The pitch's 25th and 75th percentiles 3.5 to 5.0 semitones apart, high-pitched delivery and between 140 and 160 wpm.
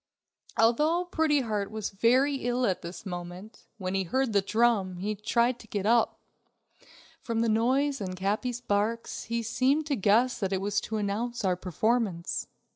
No: average, 3.8 semitones; high, 220 Hz; average, 170 wpm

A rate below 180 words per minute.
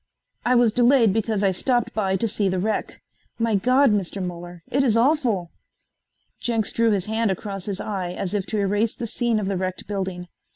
No: average, 200 wpm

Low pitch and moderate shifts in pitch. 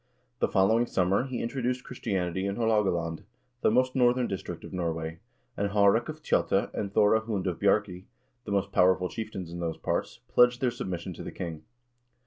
Yes: low, 100 Hz; average, 4.7 semitones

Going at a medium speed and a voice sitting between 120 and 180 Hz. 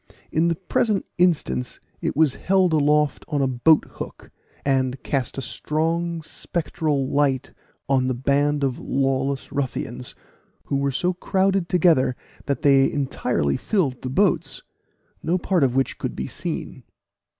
Yes: average, 145 wpm; medium, 140 Hz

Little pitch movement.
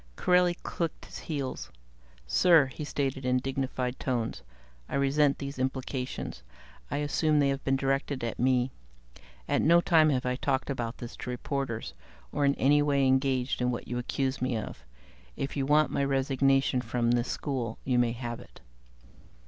Yes: narrow, 2.1 semitones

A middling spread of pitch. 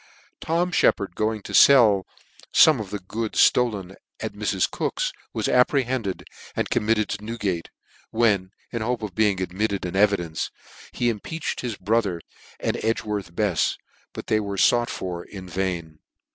Yes: average, 3.5 semitones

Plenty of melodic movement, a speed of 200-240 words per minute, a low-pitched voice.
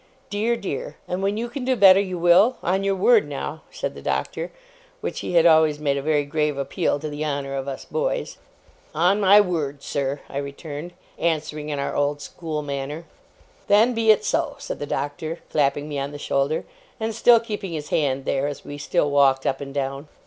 No: wide, 5.7 semitones; fast, 205 wpm; medium, 155 Hz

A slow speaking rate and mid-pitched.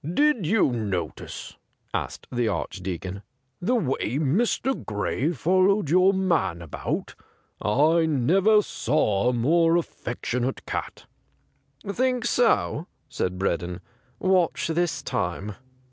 Yes: slow, 130 wpm; medium, 150 Hz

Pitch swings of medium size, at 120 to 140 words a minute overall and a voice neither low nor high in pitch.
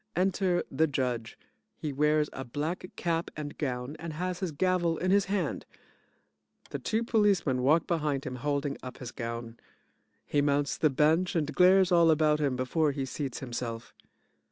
No: average, 4.7 semitones; average, 165 wpm; medium, 150 Hz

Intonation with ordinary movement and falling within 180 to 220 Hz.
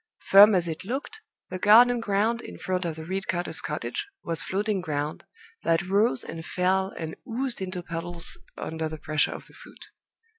Yes: average, 4.1 semitones; medium, 185 Hz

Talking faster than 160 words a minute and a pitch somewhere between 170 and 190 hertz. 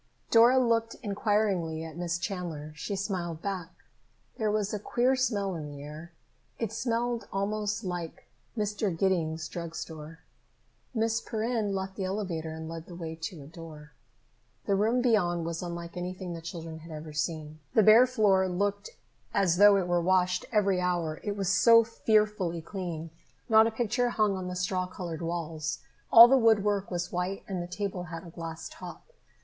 Yes: average, 175 wpm; medium, 185 Hz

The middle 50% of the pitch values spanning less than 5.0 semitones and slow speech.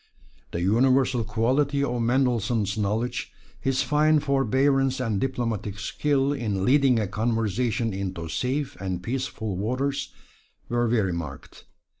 Yes: average, 4.3 semitones; slow, 120 wpm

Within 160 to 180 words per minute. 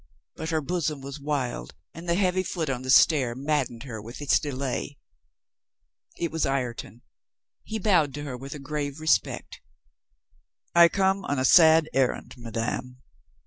Yes: average, 165 wpm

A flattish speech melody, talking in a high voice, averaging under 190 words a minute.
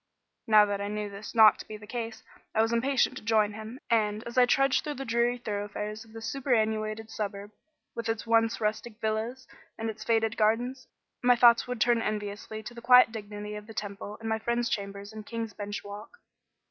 No: narrow, 2.0 semitones; high, 220 Hz; fast, 205 wpm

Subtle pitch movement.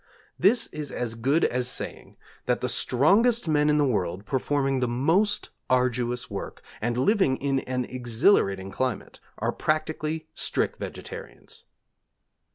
No: average, 4.2 semitones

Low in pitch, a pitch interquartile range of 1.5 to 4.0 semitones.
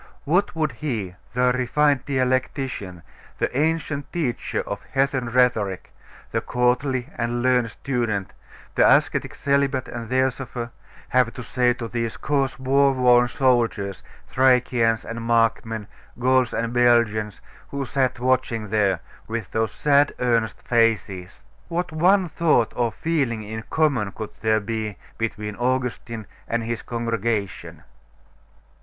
Yes: low, 120 Hz; average, 2.8 semitones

